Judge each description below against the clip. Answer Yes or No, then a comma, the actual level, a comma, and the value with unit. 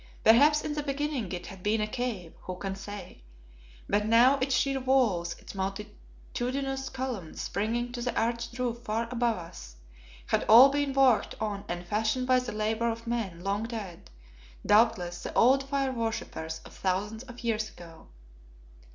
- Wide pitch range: No, average, 4.3 semitones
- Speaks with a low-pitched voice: No, high, 230 Hz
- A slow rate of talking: No, average, 165 wpm